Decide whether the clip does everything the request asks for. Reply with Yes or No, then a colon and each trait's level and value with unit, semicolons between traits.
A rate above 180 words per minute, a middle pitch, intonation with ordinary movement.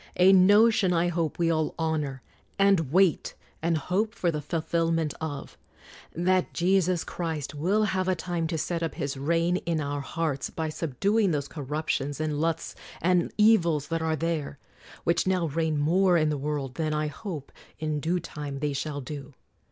No: average, 175 wpm; medium, 165 Hz; average, 3.1 semitones